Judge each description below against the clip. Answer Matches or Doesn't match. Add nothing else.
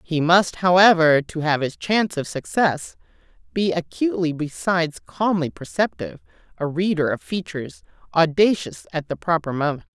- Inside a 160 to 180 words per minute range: Doesn't match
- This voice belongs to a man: Doesn't match